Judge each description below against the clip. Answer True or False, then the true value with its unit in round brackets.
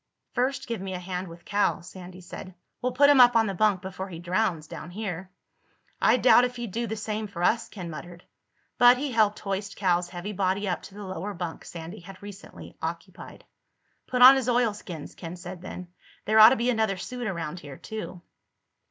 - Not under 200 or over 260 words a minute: True (205 wpm)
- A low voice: False (195 Hz)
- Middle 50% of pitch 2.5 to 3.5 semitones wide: False (3.9 semitones)